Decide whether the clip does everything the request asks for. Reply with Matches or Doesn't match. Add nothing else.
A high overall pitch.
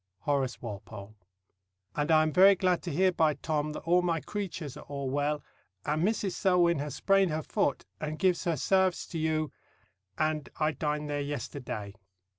Doesn't match